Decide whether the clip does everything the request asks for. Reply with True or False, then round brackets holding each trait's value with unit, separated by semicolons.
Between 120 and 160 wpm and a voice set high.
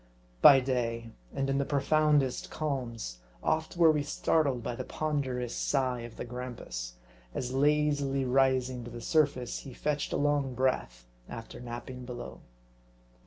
False (145 wpm; 130 Hz)